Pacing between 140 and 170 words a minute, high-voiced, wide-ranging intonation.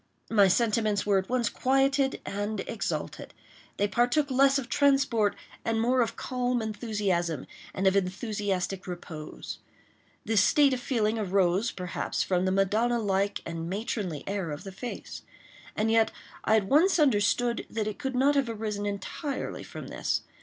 No: average, 150 wpm; high, 215 Hz; average, 4.1 semitones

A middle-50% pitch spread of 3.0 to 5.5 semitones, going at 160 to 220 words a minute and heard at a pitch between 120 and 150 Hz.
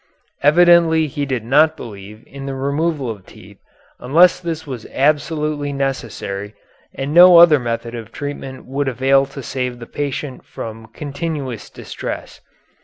No: average, 3.9 semitones; average, 145 wpm; medium, 140 Hz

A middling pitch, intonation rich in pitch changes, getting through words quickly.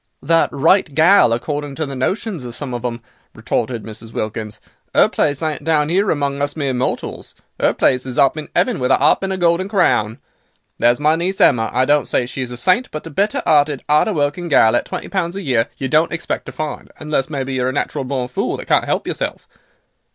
No: medium, 145 Hz; average, 4.4 semitones; fast, 225 wpm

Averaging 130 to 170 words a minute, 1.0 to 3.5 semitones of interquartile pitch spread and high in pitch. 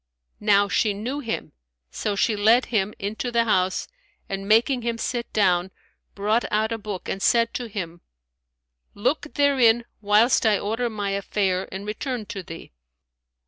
Yes: average, 155 wpm; average, 2.8 semitones; high, 215 Hz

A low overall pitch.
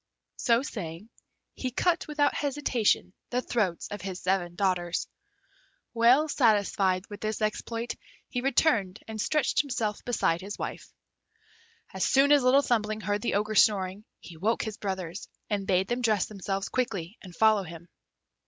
No: high, 210 Hz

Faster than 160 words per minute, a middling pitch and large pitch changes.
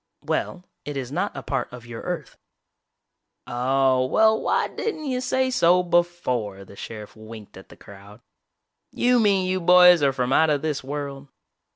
Yes: average, 170 wpm; medium, 145 Hz; wide, 6.9 semitones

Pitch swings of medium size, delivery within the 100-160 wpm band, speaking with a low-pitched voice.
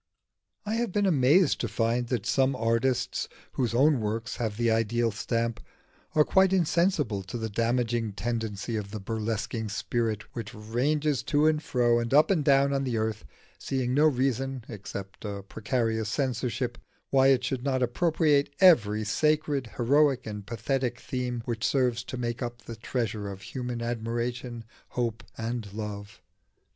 Yes: average, 3.3 semitones; average, 155 wpm; low, 120 Hz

